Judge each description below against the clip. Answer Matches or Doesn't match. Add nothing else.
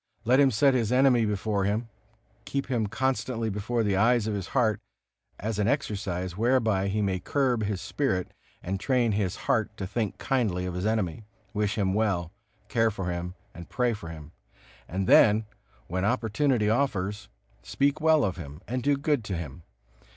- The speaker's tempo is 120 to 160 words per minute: Doesn't match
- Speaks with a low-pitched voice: Matches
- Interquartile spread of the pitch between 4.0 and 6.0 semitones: Matches